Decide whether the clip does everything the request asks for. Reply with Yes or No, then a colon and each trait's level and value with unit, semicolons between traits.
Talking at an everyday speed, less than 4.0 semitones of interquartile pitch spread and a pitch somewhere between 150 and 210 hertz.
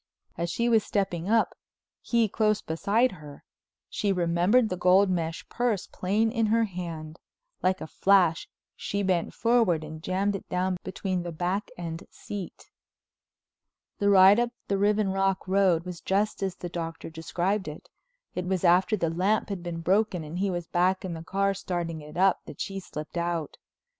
Yes: average, 175 wpm; average, 2.9 semitones; medium, 185 Hz